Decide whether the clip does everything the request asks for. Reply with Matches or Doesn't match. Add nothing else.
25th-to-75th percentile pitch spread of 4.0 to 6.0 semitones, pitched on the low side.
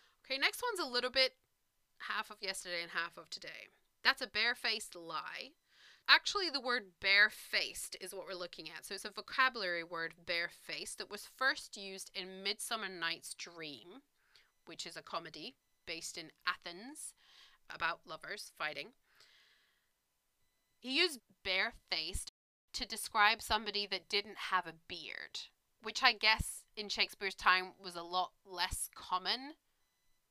Doesn't match